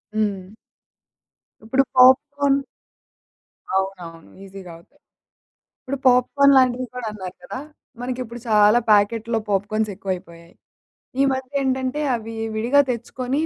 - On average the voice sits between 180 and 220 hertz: No, high, 230 Hz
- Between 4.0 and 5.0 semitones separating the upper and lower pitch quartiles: Yes, average, 4.6 semitones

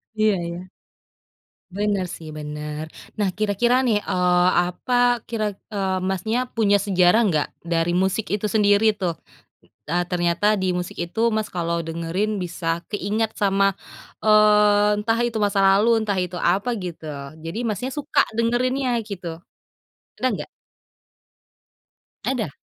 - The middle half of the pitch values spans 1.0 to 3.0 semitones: No, average, 3.4 semitones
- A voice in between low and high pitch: No, high, 200 Hz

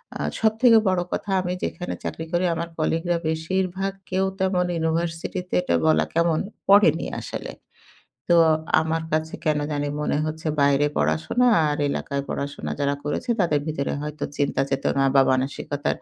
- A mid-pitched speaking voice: Yes, medium, 160 Hz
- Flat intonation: No, average, 3.8 semitones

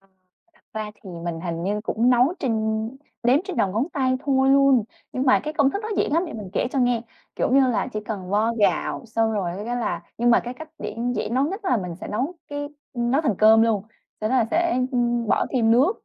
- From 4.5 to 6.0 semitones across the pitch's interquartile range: No, average, 4.0 semitones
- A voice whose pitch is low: No, high, 240 Hz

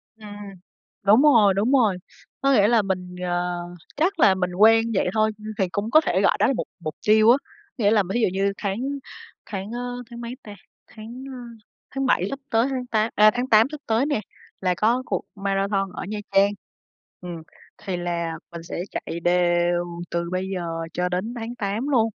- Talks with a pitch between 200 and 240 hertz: Yes, high, 210 Hz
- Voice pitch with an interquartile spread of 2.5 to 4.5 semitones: Yes, average, 4.2 semitones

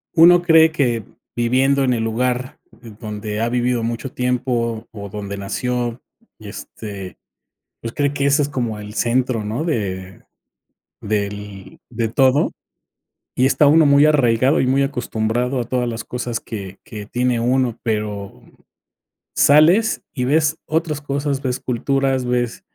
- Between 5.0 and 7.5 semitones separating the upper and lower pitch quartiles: No, average, 3.7 semitones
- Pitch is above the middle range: No, low, 125 Hz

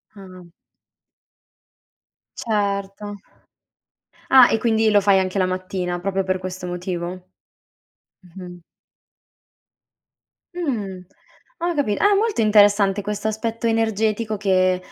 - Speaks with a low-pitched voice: No, high, 200 Hz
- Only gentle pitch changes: No, average, 3.0 semitones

